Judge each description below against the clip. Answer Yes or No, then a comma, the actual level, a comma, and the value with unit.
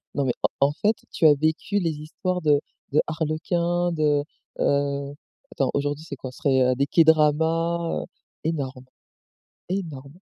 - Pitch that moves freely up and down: No, average, 2.8 semitones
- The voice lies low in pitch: No, medium, 155 Hz